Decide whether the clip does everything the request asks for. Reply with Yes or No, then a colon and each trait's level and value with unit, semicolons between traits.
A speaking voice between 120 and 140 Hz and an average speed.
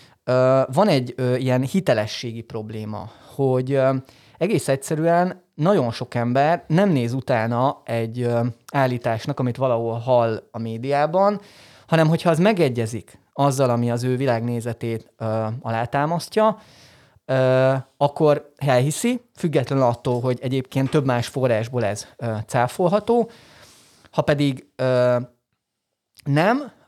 Yes: low, 130 Hz; average, 120 wpm